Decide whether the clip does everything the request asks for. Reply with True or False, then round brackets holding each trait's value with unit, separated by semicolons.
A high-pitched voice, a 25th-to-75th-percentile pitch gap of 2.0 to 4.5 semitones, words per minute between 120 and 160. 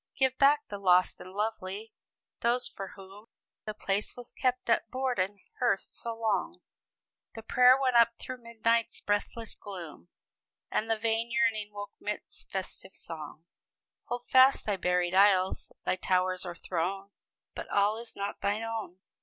True (210 Hz; 3.5 semitones; 155 wpm)